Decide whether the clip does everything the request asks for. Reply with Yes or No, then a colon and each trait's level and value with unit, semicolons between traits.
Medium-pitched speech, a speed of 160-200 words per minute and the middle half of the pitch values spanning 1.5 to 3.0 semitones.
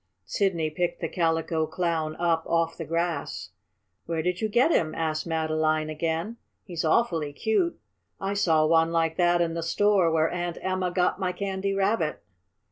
Yes: medium, 170 Hz; average, 165 wpm; narrow, 2.5 semitones